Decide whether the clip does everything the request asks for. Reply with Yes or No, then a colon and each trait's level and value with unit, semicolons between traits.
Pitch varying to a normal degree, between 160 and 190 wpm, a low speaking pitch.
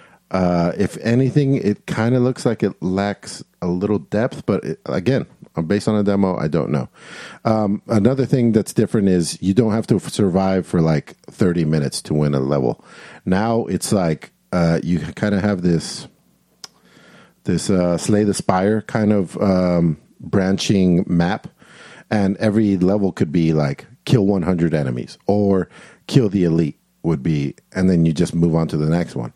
Yes: average, 3.8 semitones; average, 180 wpm; very low, 95 Hz